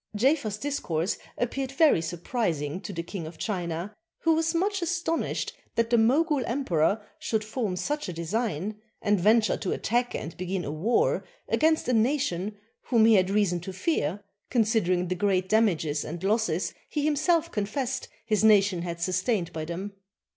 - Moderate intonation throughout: No, wide, 5.9 semitones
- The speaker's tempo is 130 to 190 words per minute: Yes, average, 160 wpm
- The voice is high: Yes, high, 210 Hz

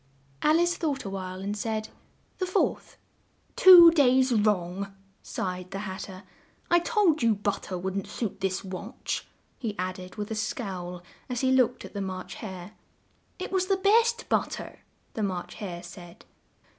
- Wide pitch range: Yes, wide, 6.4 semitones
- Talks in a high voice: Yes, high, 205 Hz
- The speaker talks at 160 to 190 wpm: Yes, average, 170 wpm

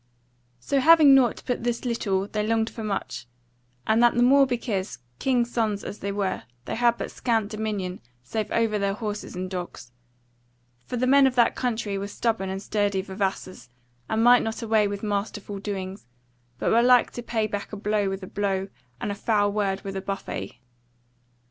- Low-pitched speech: No, high, 210 Hz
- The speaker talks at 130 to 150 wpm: No, average, 185 wpm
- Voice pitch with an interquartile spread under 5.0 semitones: Yes, average, 3.0 semitones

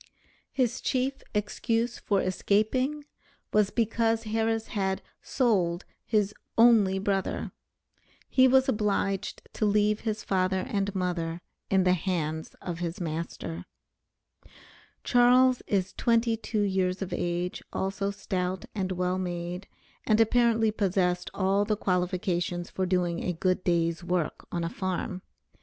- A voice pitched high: Yes, high, 195 Hz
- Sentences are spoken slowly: Yes, slow, 130 wpm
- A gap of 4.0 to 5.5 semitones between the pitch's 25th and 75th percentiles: No, average, 3.6 semitones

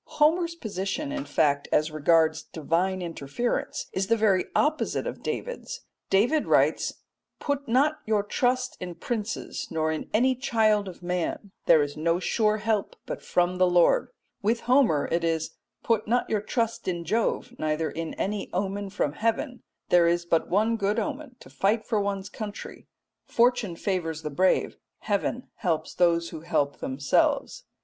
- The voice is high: Yes, high, 200 Hz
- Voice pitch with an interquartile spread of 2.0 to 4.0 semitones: No, wide, 5.6 semitones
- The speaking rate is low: No, average, 160 wpm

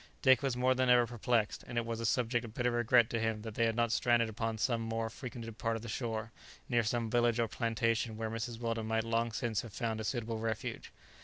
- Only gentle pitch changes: Yes, narrow, 1.1 semitones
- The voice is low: Yes, low, 115 Hz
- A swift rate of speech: Yes, fast, 240 wpm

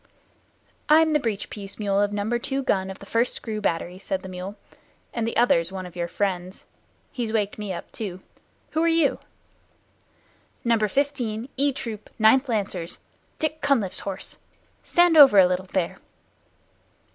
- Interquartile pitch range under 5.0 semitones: No, wide, 5.5 semitones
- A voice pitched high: Yes, high, 215 Hz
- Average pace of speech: Yes, average, 160 wpm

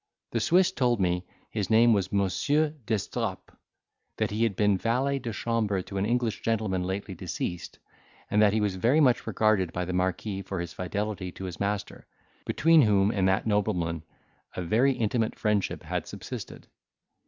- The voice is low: Yes, low, 105 Hz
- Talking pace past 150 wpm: Yes, average, 170 wpm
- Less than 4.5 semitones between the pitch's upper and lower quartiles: Yes, average, 3.4 semitones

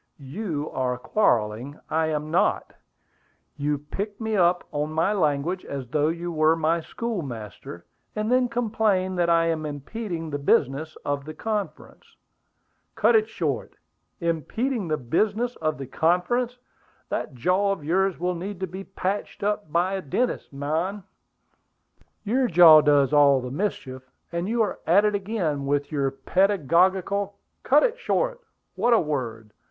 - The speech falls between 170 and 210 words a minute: No, average, 155 wpm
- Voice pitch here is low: No, medium, 170 Hz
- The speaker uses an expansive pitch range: Yes, wide, 5.8 semitones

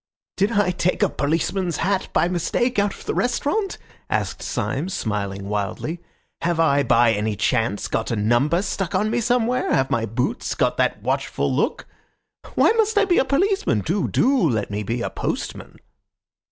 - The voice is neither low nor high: Yes, medium, 170 Hz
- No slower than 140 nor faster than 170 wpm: No, average, 180 wpm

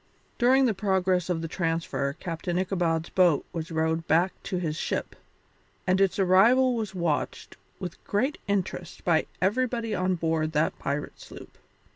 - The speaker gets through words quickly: No, average, 150 wpm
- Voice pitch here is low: No, medium, 180 Hz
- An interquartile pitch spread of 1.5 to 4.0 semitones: Yes, average, 3.3 semitones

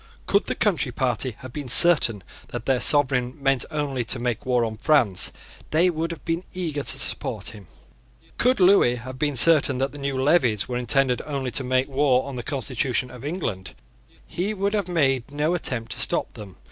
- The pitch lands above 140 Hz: No, low, 135 Hz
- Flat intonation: No, average, 3.9 semitones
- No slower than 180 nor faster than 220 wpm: Yes, average, 195 wpm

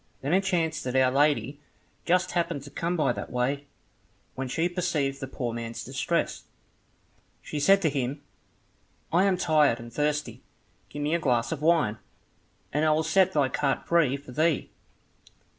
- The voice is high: No, medium, 150 Hz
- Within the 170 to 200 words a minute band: Yes, average, 175 wpm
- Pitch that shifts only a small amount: No, average, 4.0 semitones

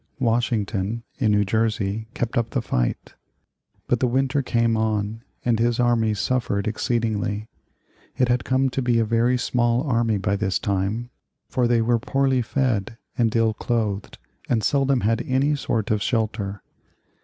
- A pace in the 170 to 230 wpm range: No, average, 155 wpm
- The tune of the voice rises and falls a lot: No, narrow, 2.4 semitones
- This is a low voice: Yes, low, 115 Hz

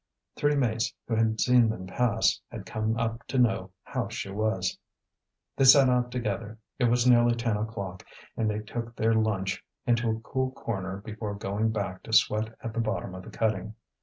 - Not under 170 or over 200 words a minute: Yes, average, 190 wpm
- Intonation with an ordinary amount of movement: No, narrow, 2.2 semitones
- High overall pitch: No, low, 110 Hz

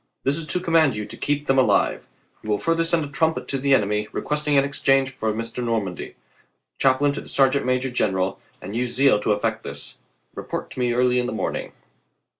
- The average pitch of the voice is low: Yes, low, 130 Hz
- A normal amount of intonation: Yes, average, 3.9 semitones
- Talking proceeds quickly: Yes, fast, 215 wpm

